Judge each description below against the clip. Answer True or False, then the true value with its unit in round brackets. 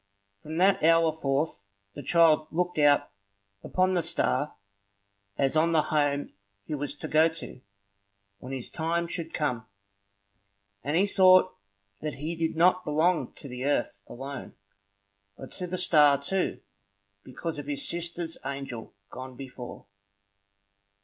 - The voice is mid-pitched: True (155 Hz)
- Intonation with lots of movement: False (3.3 semitones)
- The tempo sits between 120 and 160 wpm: True (140 wpm)